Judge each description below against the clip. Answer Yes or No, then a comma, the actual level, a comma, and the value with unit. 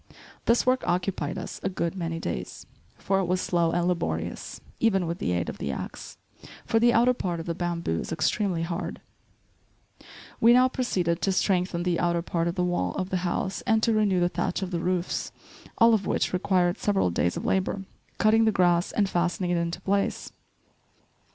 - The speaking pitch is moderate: Yes, medium, 180 Hz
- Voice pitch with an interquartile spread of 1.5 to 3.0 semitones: Yes, average, 2.7 semitones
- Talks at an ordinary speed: Yes, average, 195 wpm